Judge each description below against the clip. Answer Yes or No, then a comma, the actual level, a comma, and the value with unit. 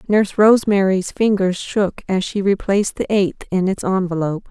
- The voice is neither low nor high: No, high, 195 Hz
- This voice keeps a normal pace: Yes, average, 160 wpm